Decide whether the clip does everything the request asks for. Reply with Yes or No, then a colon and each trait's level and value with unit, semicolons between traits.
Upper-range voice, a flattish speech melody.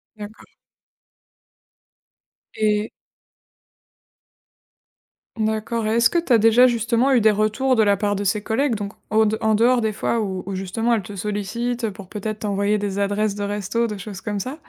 Yes: high, 215 Hz; narrow, 2.2 semitones